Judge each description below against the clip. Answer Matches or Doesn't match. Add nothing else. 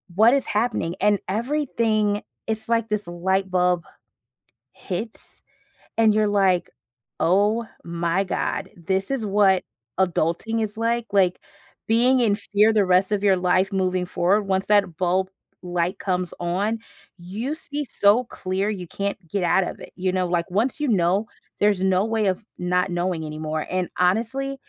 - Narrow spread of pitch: Doesn't match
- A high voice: Matches